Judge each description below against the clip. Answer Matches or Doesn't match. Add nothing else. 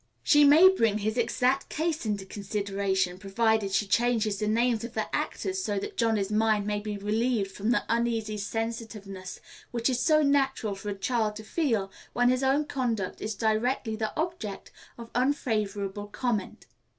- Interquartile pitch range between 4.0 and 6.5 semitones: Doesn't match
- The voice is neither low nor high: Doesn't match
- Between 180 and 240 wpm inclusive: Doesn't match